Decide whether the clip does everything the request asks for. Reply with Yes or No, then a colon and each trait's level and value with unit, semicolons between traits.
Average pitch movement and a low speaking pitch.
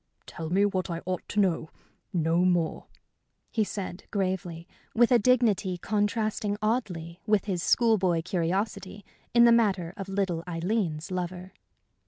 No: average, 3.3 semitones; high, 190 Hz